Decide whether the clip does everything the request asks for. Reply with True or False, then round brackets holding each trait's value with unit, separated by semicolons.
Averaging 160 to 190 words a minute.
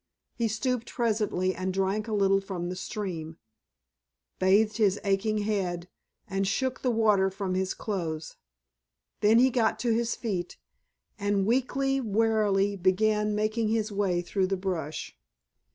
False (140 wpm)